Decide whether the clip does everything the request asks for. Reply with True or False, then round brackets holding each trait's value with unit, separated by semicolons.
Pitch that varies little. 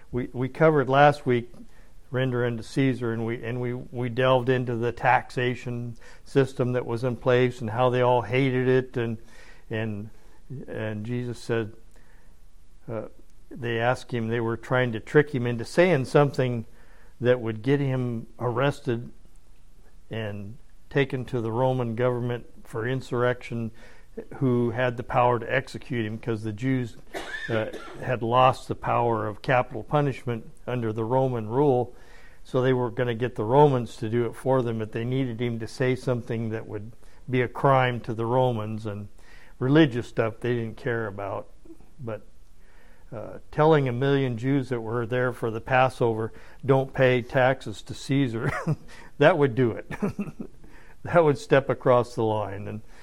True (2.2 semitones)